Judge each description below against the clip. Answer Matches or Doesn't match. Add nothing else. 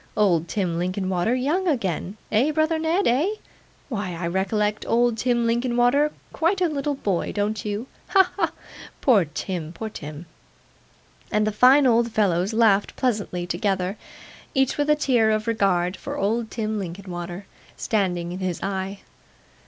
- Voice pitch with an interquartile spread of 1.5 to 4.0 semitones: Doesn't match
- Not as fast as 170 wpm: Matches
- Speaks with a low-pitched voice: Doesn't match